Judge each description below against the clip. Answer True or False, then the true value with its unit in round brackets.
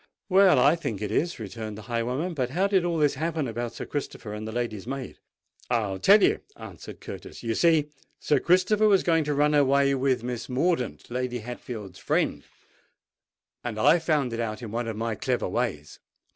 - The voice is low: True (125 Hz)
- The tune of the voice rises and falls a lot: True (5.8 semitones)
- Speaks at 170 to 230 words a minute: True (190 wpm)